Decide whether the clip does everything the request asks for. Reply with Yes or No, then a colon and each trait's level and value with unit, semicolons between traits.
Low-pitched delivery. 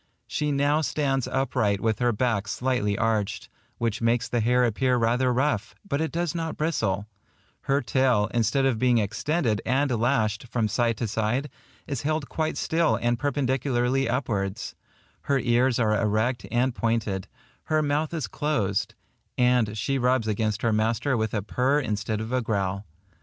Yes: low, 120 Hz